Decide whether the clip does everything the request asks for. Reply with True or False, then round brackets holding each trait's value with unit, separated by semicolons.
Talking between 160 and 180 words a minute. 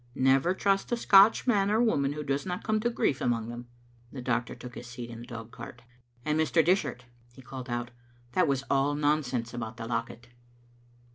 False (200 wpm)